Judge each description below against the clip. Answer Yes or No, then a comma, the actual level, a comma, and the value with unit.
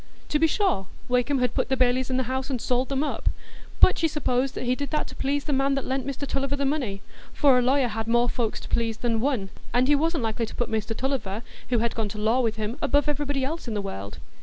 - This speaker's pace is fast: Yes, fast, 260 wpm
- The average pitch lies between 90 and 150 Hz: No, very high, 255 Hz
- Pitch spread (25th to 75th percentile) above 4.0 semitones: No, average, 3.5 semitones